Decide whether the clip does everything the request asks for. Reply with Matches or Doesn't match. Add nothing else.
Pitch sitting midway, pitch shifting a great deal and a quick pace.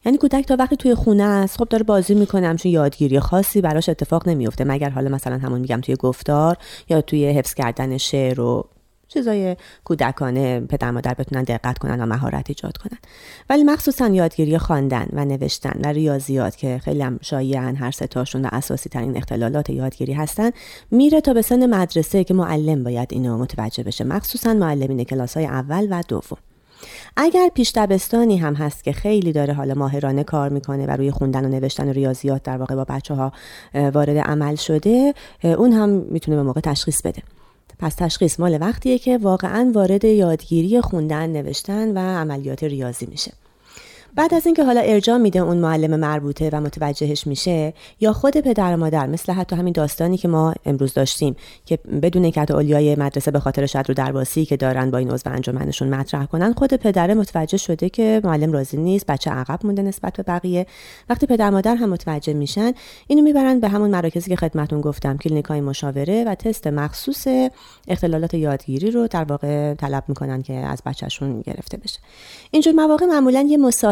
Matches